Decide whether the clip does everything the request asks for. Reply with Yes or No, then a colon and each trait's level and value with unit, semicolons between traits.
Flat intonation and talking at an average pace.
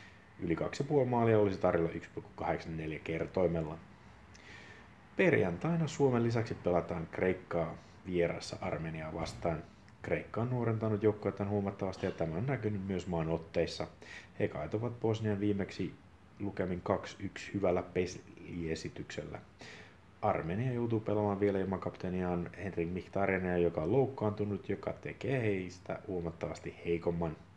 No: average, 3.8 semitones; average, 110 wpm